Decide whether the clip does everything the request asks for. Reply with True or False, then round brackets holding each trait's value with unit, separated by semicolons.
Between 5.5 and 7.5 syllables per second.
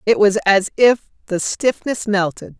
False (4.4 syllables/s)